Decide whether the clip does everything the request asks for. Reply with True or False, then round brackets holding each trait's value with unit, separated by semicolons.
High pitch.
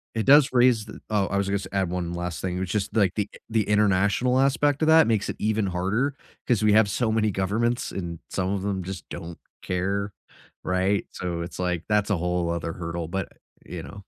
False (100 Hz)